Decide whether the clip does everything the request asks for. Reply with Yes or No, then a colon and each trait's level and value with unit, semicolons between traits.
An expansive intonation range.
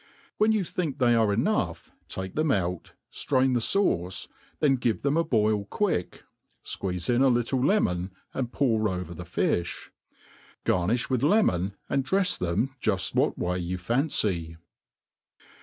Yes: wide, 7.2 semitones